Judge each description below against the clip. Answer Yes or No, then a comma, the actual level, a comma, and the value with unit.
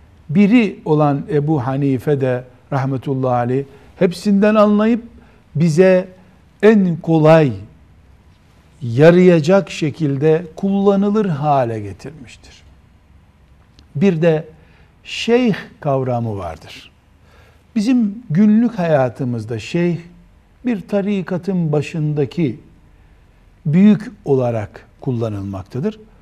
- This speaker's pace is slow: Yes, slow, 75 wpm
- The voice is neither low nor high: Yes, medium, 145 Hz